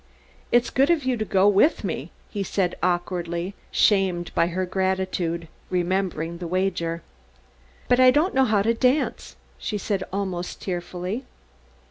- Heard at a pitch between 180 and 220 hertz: Yes, high, 190 Hz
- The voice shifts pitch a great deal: No, average, 3.6 semitones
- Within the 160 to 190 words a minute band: No, average, 145 wpm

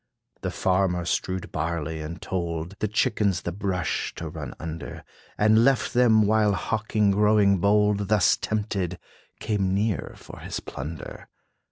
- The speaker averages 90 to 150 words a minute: Yes, average, 140 wpm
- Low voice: Yes, low, 100 Hz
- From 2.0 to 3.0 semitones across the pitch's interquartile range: No, average, 3.6 semitones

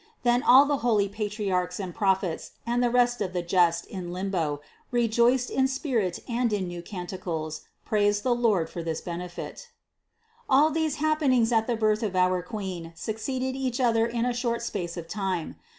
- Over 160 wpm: Yes, average, 180 wpm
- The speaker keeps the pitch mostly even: No, average, 5.2 semitones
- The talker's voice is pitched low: No, high, 215 Hz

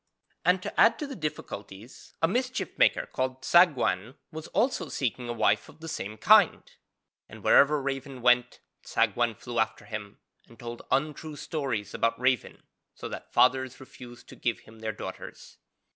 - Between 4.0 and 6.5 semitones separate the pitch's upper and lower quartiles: Yes, average, 4.8 semitones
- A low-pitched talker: Yes, low, 130 Hz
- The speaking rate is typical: Yes, average, 160 wpm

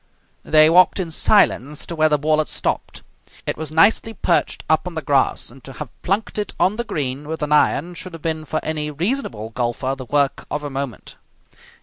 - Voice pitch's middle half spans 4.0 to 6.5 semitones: No, average, 3.3 semitones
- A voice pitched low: No, medium, 155 Hz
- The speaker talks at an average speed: No, fast, 215 wpm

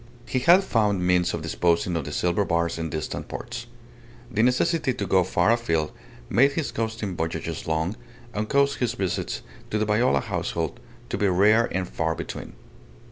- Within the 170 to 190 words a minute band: Yes, average, 175 wpm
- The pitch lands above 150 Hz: No, low, 100 Hz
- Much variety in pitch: Yes, wide, 5.7 semitones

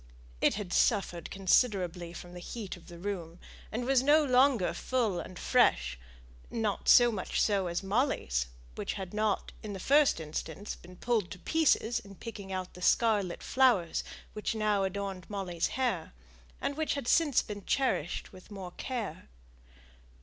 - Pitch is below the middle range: No, high, 200 Hz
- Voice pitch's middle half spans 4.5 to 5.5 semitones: Yes, average, 5.1 semitones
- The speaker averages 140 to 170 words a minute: Yes, average, 160 wpm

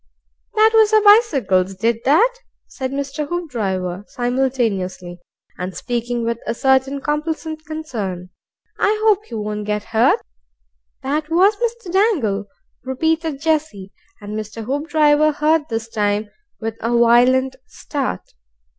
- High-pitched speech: Yes, very high, 260 Hz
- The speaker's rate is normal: No, slow, 125 wpm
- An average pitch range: No, wide, 6.5 semitones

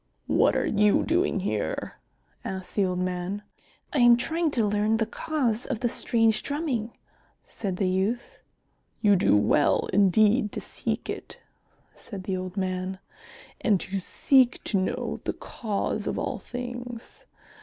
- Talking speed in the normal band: Yes, average, 150 wpm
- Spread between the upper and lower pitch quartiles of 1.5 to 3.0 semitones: No, average, 4.3 semitones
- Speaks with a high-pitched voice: Yes, high, 210 Hz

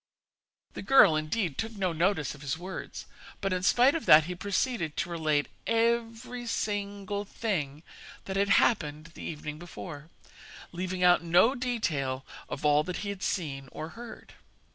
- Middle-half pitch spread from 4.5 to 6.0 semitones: Yes, wide, 5.4 semitones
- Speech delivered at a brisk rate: No, average, 160 wpm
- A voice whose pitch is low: No, medium, 180 Hz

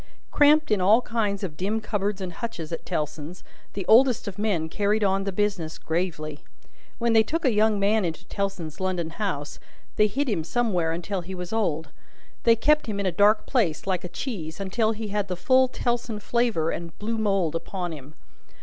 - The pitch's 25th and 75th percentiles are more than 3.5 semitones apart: Yes, average, 4.3 semitones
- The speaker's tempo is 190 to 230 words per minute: Yes, average, 195 wpm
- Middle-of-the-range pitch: No, high, 200 Hz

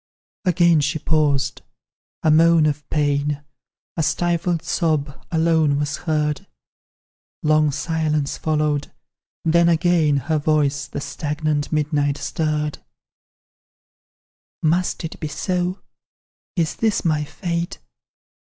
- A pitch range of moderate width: No, narrow, 2.2 semitones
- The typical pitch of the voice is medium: Yes, medium, 155 Hz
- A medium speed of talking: No, slow, 105 wpm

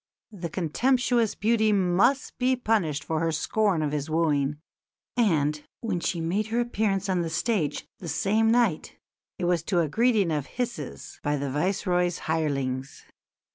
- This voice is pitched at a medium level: Yes, medium, 180 Hz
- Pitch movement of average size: No, wide, 6.0 semitones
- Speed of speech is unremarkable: Yes, average, 155 wpm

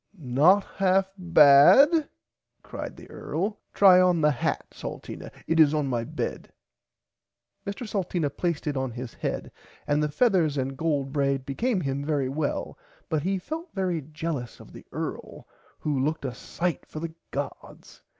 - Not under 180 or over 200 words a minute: No, average, 160 wpm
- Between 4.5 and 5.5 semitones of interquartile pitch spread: Yes, average, 4.8 semitones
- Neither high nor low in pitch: Yes, medium, 155 Hz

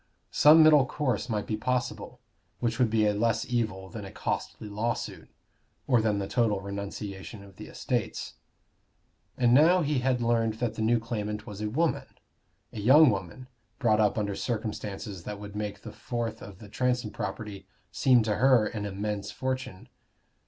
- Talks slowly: No, average, 170 wpm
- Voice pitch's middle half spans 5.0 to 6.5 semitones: No, average, 3.2 semitones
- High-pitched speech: No, low, 110 Hz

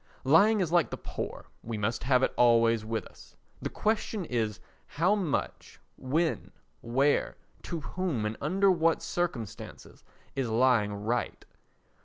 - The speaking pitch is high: No, low, 130 Hz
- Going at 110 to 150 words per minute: Yes, average, 140 wpm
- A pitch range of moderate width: No, wide, 7.1 semitones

